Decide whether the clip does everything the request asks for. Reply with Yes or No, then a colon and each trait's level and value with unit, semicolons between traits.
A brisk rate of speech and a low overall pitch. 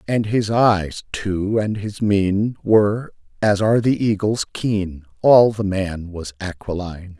No: average, 150 wpm; low, 100 Hz